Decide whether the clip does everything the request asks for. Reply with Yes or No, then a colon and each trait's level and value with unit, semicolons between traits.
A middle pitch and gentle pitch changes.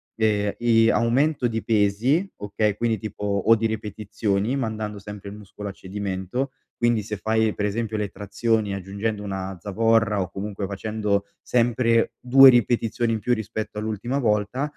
No: low, 110 Hz; narrow, 2.2 semitones